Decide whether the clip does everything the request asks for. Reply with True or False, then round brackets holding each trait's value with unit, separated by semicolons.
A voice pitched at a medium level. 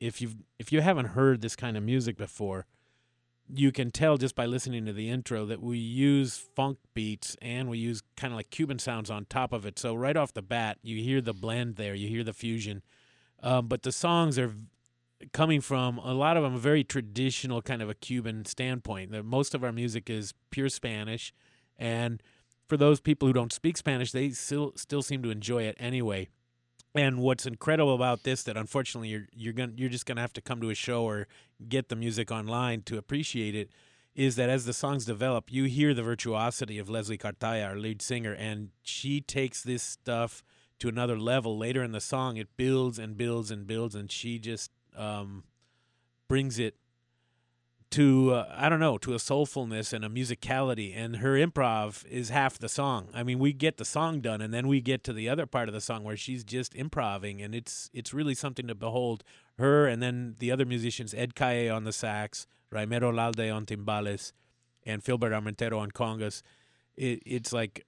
False (120 Hz)